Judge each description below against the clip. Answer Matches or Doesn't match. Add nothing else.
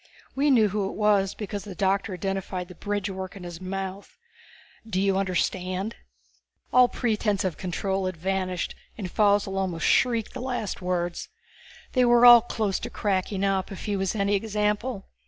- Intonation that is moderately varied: Doesn't match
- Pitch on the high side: Matches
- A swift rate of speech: Doesn't match